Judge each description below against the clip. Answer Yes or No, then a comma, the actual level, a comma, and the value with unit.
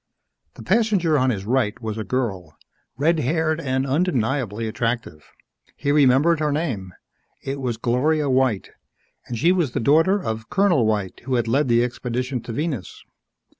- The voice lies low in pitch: Yes, low, 130 Hz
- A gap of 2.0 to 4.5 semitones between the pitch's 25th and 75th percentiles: No, average, 5.1 semitones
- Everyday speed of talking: Yes, average, 160 wpm